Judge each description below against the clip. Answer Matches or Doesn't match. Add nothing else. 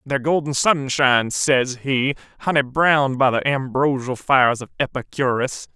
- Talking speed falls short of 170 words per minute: Matches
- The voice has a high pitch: Doesn't match